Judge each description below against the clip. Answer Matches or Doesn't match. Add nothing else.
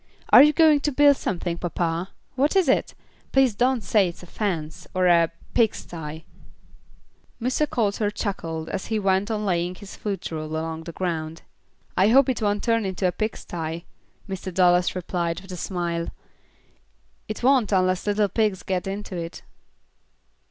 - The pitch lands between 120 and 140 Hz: Doesn't match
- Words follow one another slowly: Doesn't match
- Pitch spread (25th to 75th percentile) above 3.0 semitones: Matches